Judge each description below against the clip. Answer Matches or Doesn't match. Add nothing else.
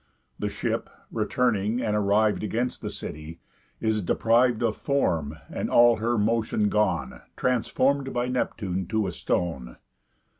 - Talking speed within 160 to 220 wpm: Doesn't match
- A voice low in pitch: Matches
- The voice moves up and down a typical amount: Matches